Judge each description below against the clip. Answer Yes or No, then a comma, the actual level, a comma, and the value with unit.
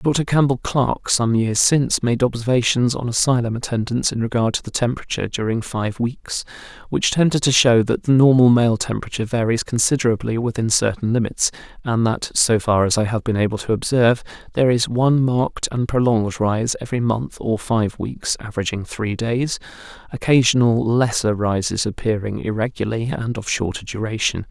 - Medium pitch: No, low, 115 Hz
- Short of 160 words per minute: No, average, 165 wpm